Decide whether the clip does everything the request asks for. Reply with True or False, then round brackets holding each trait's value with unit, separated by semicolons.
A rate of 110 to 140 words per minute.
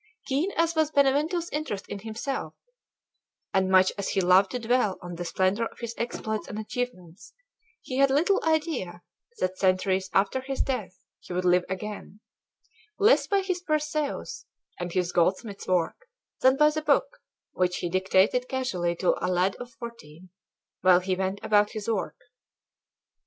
False (160 wpm)